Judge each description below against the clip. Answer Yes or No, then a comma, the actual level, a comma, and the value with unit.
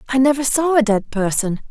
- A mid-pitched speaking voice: No, high, 245 Hz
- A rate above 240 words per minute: No, fast, 210 wpm